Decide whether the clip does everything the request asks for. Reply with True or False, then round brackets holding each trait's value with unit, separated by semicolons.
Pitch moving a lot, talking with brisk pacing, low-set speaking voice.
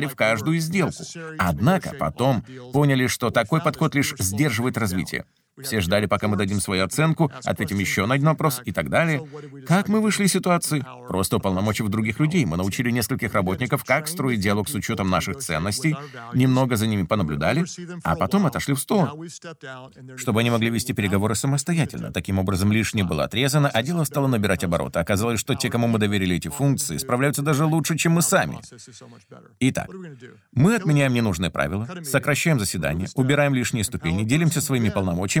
True (6.6 semitones; 170 wpm; 130 Hz)